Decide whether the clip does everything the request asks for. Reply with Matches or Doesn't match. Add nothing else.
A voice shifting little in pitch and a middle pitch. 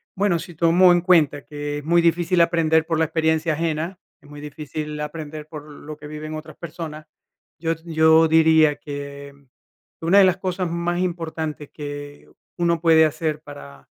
Matches